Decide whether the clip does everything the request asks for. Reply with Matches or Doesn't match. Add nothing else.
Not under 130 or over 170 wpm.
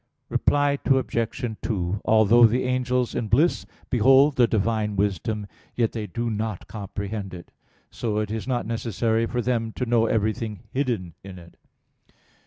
Matches